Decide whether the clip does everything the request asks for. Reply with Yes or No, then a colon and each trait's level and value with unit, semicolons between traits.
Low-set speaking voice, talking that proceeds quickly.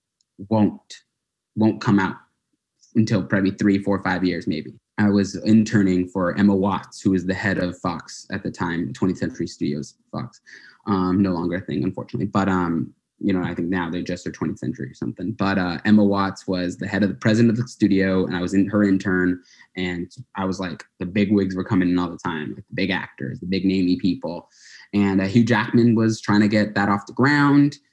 Yes: very low, 95 Hz; fast, 220 wpm